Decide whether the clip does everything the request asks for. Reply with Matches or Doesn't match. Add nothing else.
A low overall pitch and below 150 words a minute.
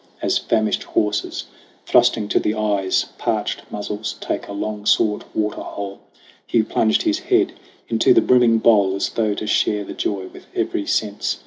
Doesn't match